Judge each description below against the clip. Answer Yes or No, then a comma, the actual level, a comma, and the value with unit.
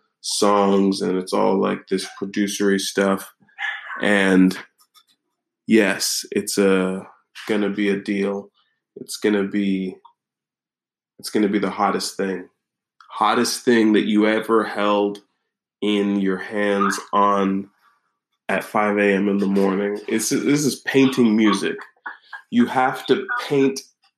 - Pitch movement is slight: Yes, narrow, 2.2 semitones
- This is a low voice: Yes, low, 100 Hz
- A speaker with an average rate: No, slow, 125 wpm